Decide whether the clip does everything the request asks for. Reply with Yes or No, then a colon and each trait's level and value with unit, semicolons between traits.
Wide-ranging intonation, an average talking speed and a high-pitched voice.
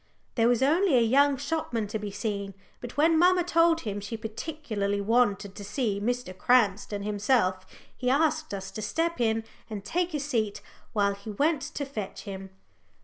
Yes: wide, 6.2 semitones; average, 175 wpm; high, 230 Hz